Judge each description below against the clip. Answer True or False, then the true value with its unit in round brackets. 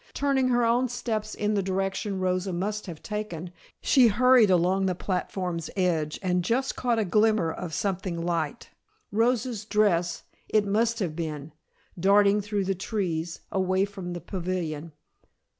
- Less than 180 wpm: True (150 wpm)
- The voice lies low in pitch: False (195 Hz)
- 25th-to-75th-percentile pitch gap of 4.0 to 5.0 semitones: False (3.5 semitones)